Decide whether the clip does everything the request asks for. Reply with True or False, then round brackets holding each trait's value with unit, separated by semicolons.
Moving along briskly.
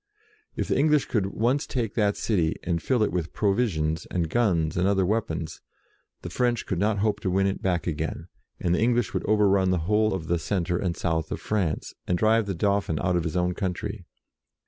True (215 wpm)